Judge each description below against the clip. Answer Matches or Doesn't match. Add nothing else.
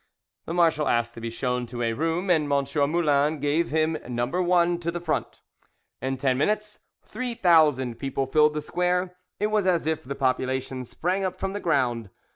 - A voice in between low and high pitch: Matches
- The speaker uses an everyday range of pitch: Matches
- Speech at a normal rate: Matches